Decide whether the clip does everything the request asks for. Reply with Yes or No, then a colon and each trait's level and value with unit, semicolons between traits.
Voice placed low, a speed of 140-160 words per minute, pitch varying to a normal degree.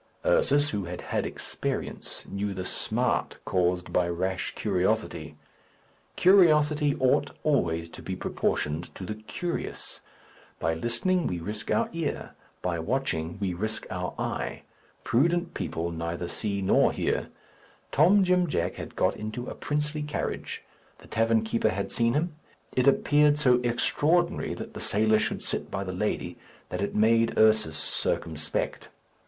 No: low, 110 Hz; average, 145 wpm; wide, 8.4 semitones